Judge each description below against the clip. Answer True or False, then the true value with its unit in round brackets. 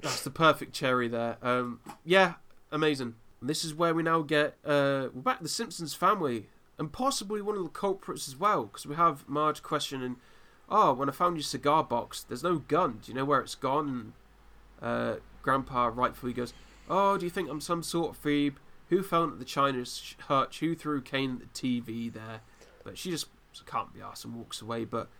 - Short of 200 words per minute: False (205 wpm)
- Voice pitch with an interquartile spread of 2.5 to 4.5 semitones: False (5.0 semitones)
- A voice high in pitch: False (140 Hz)